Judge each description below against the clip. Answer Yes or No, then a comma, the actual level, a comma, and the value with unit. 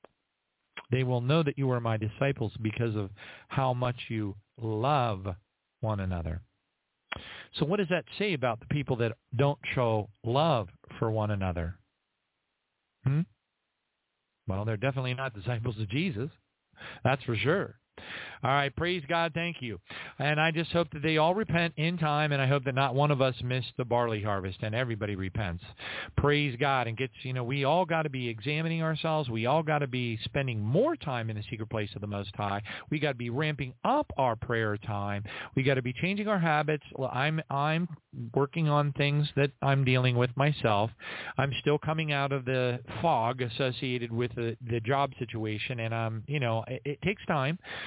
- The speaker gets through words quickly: No, average, 190 wpm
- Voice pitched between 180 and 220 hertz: No, low, 130 Hz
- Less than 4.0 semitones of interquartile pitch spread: No, average, 4.6 semitones